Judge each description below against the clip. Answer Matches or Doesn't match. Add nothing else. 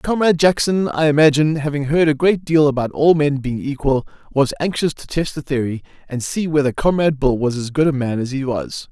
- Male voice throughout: Matches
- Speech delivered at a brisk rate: Matches